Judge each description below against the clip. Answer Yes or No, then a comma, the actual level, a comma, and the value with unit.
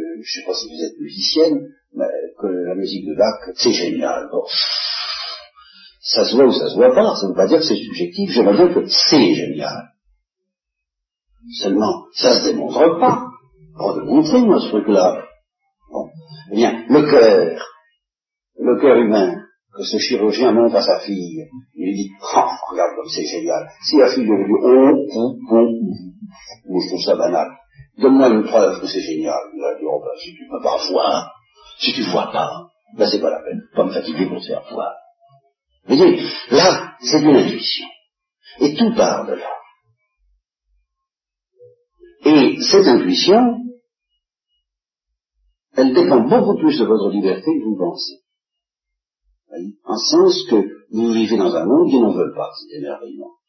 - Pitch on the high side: Yes, very high, 265 Hz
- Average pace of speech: Yes, average, 175 wpm